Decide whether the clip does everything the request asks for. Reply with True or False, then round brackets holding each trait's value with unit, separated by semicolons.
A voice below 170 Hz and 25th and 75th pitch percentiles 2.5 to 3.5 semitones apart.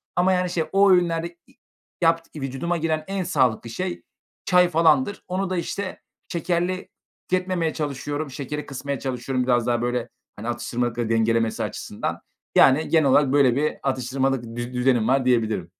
False (140 Hz; 5.6 semitones)